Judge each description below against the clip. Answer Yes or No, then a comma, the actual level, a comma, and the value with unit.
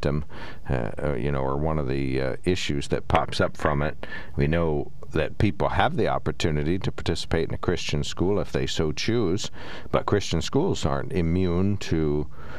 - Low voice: Yes, very low, 75 Hz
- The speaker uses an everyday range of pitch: Yes, average, 3.0 semitones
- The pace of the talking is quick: No, average, 175 wpm